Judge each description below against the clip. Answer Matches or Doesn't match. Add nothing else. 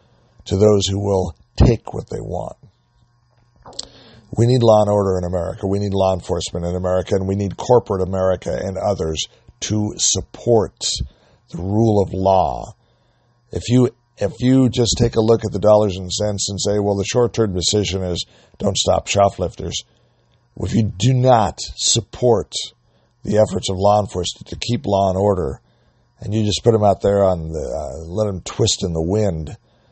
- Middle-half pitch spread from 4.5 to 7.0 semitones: Doesn't match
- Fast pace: Doesn't match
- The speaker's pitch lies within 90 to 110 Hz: Matches